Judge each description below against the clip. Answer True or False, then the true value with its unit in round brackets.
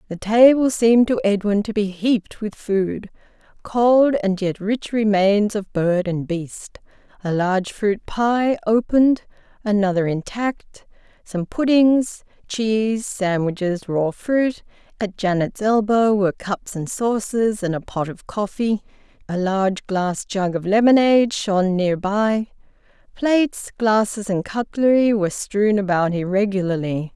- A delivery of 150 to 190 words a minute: False (135 wpm)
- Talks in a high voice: True (205 Hz)